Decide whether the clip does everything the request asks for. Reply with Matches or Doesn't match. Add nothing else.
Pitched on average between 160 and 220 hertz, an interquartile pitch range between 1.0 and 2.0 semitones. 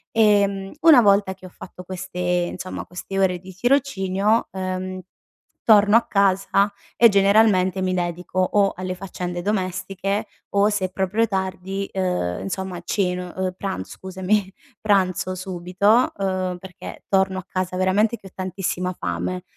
Matches